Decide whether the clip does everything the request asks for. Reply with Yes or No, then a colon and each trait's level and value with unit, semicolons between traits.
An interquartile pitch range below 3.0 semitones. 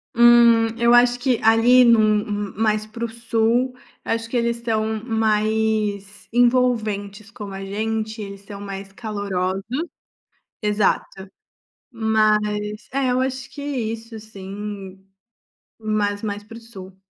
Yes: narrow, 2.4 semitones